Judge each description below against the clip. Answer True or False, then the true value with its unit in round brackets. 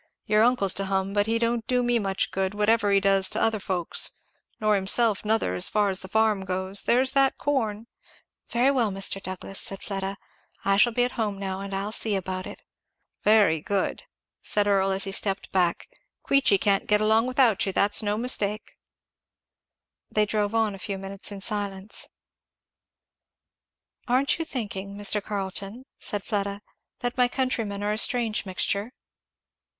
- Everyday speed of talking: True (170 wpm)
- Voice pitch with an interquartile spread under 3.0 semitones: True (2.5 semitones)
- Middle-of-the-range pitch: False (205 Hz)